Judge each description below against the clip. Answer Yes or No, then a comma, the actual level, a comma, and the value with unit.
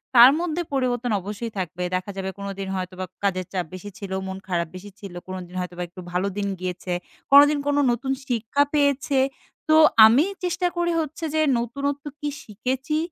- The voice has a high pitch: Yes, high, 225 Hz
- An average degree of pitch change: No, wide, 7.2 semitones